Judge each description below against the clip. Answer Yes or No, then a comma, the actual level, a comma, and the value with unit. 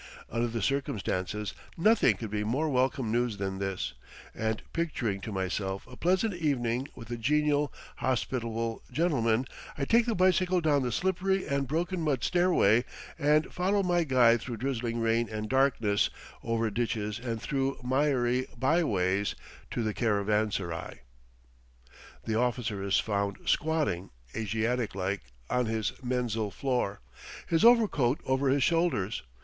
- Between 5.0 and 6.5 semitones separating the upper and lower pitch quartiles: Yes, average, 5.3 semitones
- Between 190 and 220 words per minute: No, average, 140 wpm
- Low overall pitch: Yes, low, 120 Hz